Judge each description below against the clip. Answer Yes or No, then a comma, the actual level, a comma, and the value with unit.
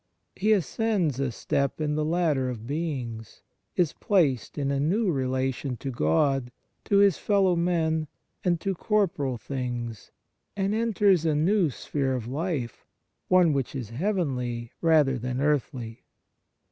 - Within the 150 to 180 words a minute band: No, average, 140 wpm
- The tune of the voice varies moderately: No, wide, 5.8 semitones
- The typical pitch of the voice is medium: Yes, medium, 145 Hz